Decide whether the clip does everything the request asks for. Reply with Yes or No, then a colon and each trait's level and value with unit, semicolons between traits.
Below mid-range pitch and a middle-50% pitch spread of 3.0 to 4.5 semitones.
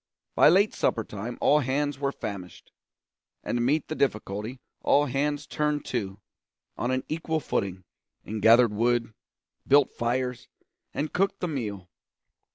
No: low, 125 Hz; average, 5.0 semitones